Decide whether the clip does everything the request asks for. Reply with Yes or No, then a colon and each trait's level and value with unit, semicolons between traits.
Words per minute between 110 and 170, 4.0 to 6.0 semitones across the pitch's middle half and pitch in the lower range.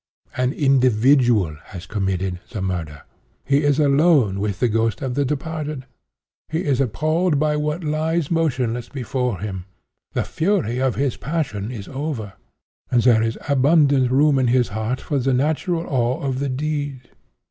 Yes: average, 160 wpm; average, 4.7 semitones; low, 130 Hz